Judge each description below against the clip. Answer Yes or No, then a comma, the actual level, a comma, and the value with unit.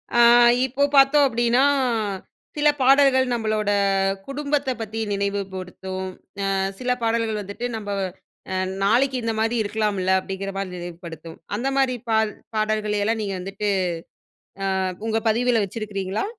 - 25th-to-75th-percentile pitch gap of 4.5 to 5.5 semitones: No, average, 3.8 semitones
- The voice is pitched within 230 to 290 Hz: No, high, 215 Hz